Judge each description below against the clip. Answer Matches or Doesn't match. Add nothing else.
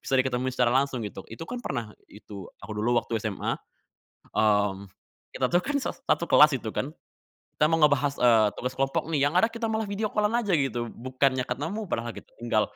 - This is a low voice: Matches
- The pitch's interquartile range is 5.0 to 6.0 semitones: Matches